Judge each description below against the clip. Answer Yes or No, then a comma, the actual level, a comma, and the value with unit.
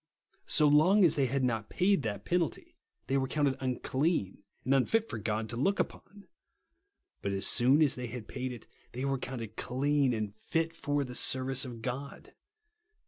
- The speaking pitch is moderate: No, low, 130 Hz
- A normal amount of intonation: Yes, average, 3.6 semitones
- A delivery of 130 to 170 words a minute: No, average, 185 wpm